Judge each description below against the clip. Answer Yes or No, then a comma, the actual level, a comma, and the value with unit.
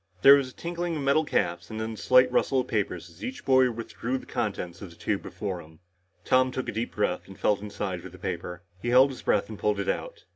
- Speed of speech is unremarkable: No, fast, 255 wpm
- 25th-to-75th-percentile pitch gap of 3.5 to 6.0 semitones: Yes, wide, 5.6 semitones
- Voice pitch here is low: Yes, low, 110 Hz